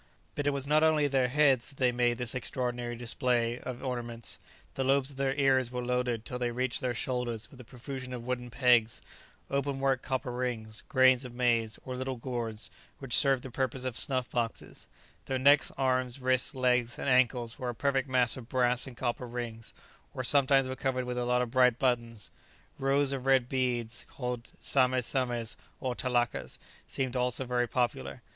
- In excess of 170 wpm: Yes, average, 190 wpm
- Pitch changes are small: Yes, narrow, 1.6 semitones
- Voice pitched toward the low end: Yes, low, 125 Hz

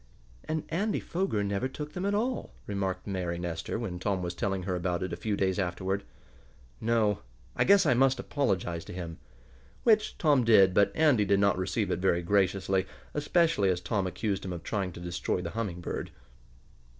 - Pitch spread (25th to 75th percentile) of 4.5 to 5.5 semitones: Yes, average, 5.2 semitones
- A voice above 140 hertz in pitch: No, low, 100 Hz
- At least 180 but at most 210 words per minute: Yes, average, 185 wpm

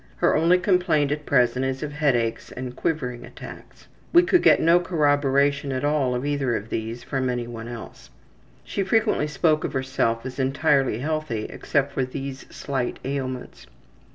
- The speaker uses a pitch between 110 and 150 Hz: Yes, low, 135 Hz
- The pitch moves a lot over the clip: No, average, 3.3 semitones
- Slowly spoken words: No, average, 165 wpm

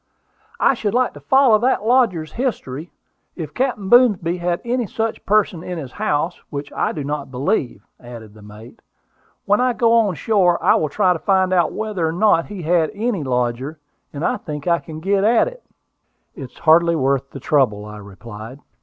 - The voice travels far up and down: Yes, wide, 7.4 semitones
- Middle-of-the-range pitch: Yes, medium, 170 Hz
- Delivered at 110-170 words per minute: No, average, 190 wpm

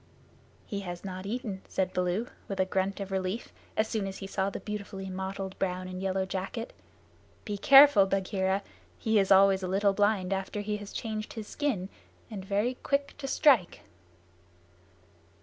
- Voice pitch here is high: Yes, high, 195 Hz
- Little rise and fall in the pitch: Yes, narrow, 2.0 semitones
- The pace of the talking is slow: No, average, 165 wpm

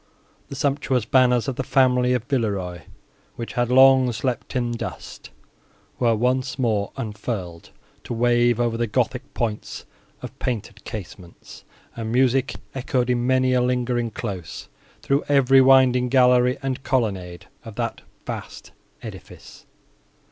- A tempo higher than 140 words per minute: No, slow, 135 wpm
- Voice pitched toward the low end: Yes, low, 125 Hz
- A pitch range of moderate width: No, narrow, 2.3 semitones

